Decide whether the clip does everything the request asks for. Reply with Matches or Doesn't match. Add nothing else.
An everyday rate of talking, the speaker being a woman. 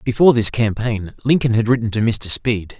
Doesn't match